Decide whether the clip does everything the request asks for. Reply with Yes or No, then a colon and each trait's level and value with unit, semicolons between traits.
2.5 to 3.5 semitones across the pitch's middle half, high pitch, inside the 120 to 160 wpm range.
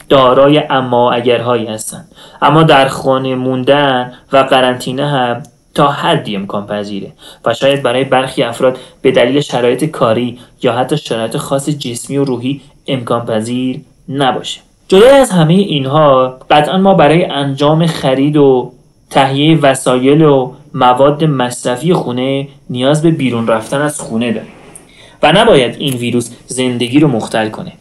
No: average, 2.8 semitones; low, 135 Hz; average, 140 wpm